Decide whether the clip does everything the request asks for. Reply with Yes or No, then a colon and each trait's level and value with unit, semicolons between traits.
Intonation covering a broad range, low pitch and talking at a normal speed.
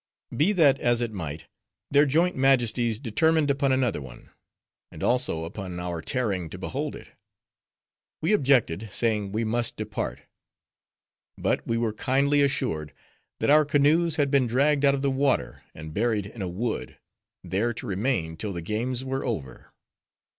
Yes: wide, 5.7 semitones; low, 120 Hz; average, 160 wpm